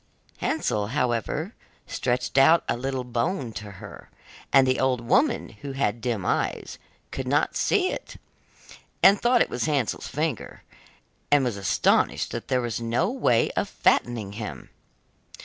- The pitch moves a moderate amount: Yes, average, 4.0 semitones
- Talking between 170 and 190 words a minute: No, average, 150 wpm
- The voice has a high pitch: No, low, 125 Hz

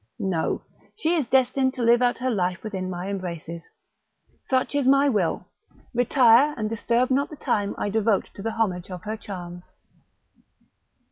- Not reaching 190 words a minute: Yes, average, 160 wpm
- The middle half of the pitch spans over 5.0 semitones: Yes, wide, 5.6 semitones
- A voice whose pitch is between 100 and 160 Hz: No, high, 225 Hz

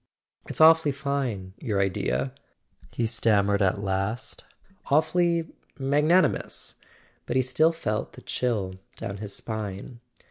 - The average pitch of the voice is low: Yes, low, 115 Hz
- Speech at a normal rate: No, slow, 110 wpm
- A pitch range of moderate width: No, wide, 6.3 semitones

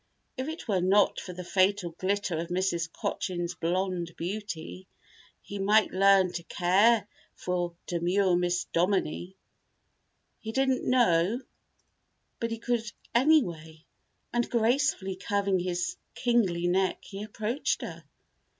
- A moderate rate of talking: No, slow, 125 wpm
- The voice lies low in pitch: No, high, 190 Hz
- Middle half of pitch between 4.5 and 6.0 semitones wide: No, average, 3.8 semitones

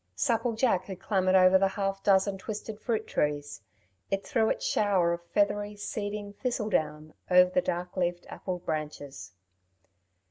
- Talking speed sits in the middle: Yes, average, 150 wpm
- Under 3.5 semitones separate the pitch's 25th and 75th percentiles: Yes, average, 3.0 semitones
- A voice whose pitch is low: No, high, 195 Hz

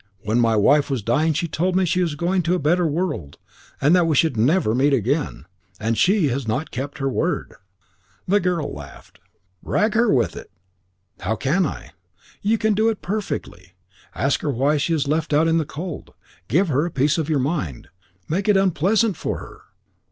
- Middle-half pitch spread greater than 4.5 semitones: Yes, average, 5.2 semitones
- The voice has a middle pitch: Yes, medium, 155 Hz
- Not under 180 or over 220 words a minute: Yes, average, 195 wpm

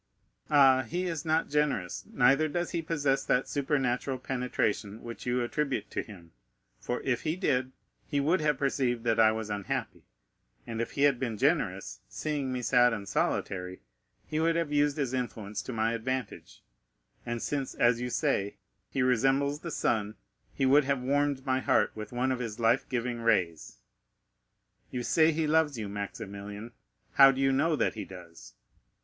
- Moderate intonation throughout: Yes, average, 4.1 semitones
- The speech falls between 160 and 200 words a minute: Yes, average, 175 wpm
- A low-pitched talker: Yes, low, 130 Hz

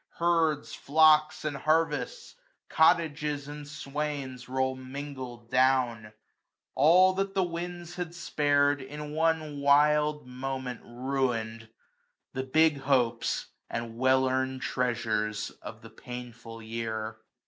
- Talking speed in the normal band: No, slow, 115 wpm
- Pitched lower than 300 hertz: Yes, medium, 140 Hz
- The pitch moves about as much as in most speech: Yes, average, 3.5 semitones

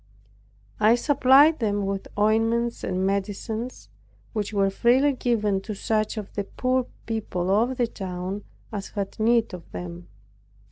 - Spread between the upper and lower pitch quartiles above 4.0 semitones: No, average, 3.4 semitones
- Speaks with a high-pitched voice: Yes, high, 215 Hz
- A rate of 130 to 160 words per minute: Yes, average, 140 wpm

